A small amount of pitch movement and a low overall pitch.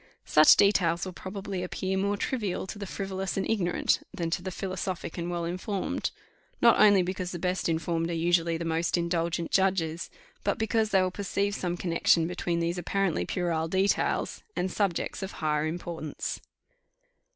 No: narrow, 2.3 semitones; medium, 180 Hz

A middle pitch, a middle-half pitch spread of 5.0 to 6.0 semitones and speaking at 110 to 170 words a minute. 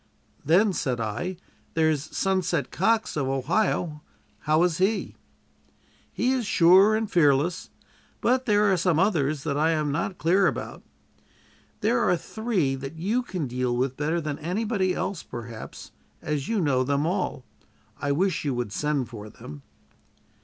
Yes: medium, 160 Hz; wide, 5.6 semitones; average, 155 wpm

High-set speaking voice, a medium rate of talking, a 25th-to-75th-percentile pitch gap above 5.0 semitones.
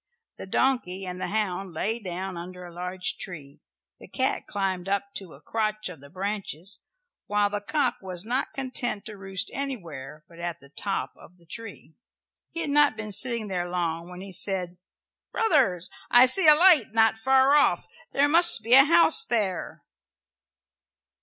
Yes: high, 200 Hz; average, 170 wpm; wide, 5.4 semitones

